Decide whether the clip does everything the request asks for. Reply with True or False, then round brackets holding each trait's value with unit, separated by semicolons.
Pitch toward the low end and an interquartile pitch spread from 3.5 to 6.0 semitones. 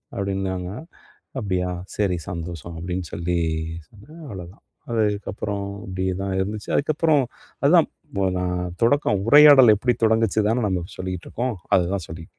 True (100 Hz; 3.8 semitones)